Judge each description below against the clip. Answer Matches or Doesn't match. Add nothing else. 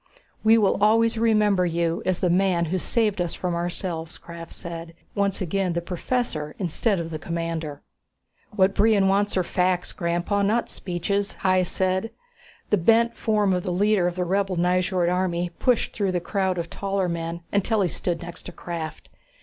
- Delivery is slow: Doesn't match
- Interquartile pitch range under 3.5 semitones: Matches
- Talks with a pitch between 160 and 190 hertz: Matches